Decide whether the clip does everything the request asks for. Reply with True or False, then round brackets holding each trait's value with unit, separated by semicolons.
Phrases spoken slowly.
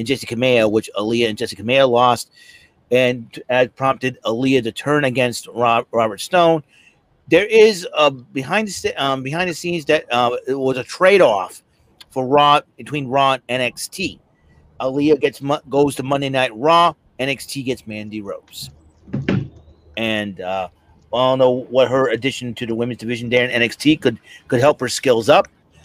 False (165 wpm)